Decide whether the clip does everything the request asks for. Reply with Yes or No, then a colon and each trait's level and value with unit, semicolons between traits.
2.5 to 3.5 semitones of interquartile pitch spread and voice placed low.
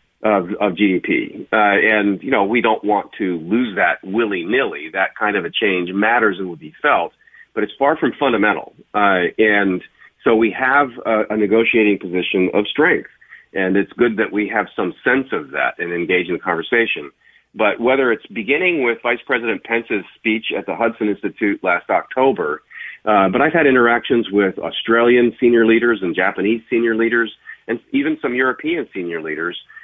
Yes: average, 2.9 semitones; low, 110 Hz